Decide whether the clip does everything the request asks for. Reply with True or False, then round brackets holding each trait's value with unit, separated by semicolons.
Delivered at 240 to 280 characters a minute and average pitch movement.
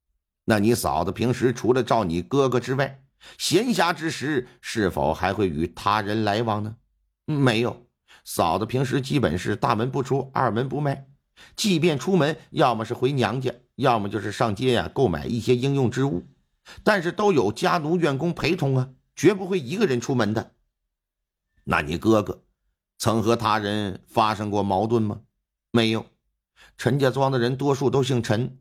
True (245 characters per minute; 4.1 semitones)